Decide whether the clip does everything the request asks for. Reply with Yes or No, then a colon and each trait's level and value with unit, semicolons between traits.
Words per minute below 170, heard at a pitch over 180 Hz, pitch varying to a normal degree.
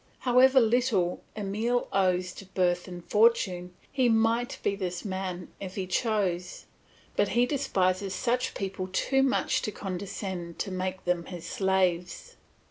Yes: average, 140 wpm; high, 190 Hz; average, 3.9 semitones